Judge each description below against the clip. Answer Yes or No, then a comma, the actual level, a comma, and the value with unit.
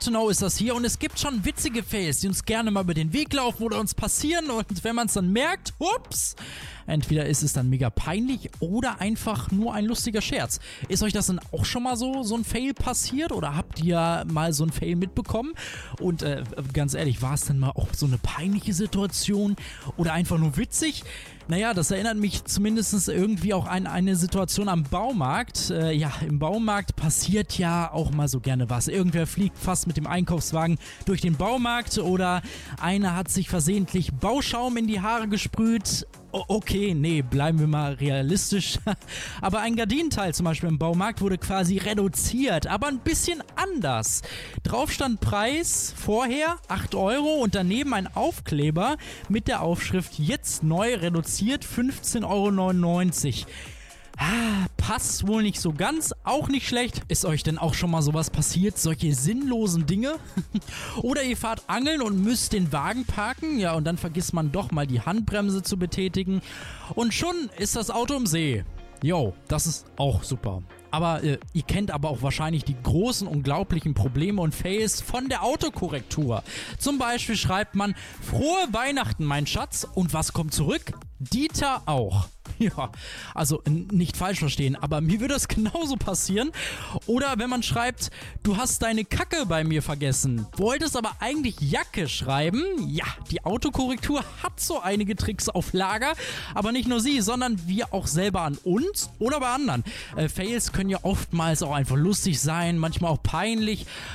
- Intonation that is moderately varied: No, wide, 6.4 semitones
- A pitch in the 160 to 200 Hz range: Yes, high, 190 Hz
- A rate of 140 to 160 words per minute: No, average, 175 wpm